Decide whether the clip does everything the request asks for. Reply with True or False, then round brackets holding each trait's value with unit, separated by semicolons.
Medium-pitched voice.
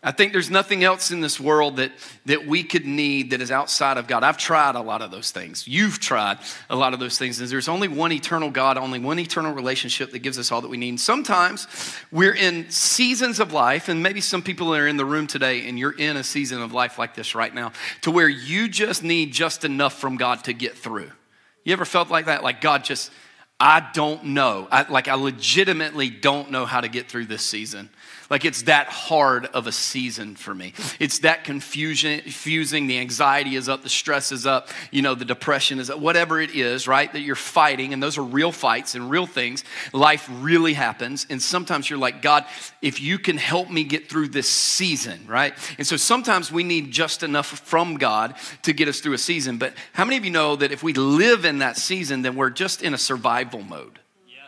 True (145 Hz)